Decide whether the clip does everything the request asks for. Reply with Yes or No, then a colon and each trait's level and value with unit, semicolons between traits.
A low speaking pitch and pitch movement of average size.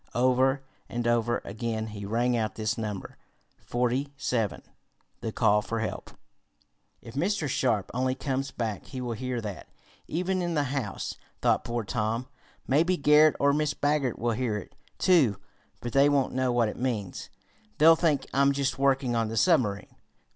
Yes: low, 125 Hz; average, 3.9 semitones